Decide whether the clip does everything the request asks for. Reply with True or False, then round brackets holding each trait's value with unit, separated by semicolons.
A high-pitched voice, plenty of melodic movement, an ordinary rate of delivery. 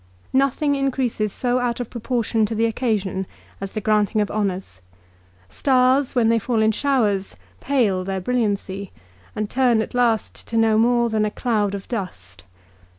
False (225 Hz; 3.4 semitones; 160 wpm)